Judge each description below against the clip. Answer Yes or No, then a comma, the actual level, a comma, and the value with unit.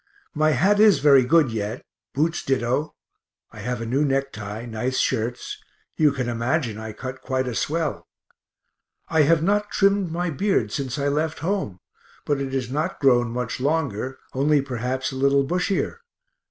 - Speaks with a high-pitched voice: No, low, 135 Hz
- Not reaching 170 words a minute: Yes, average, 160 wpm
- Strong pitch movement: No, average, 4.4 semitones